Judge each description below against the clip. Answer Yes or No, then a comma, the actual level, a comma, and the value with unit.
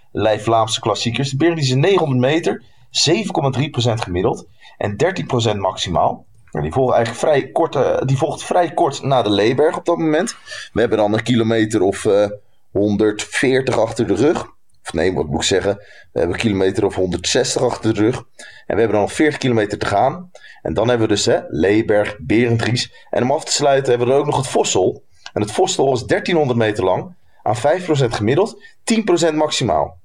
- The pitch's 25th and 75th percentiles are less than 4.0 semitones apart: No, average, 4.5 semitones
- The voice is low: Yes, low, 120 Hz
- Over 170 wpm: Yes, average, 190 wpm